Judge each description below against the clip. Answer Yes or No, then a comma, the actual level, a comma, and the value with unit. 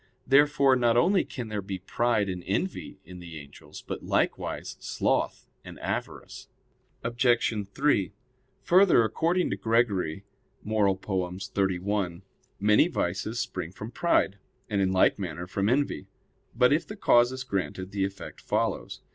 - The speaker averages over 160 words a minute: No, average, 140 wpm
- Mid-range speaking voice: No, low, 105 Hz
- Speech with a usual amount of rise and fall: Yes, average, 4.6 semitones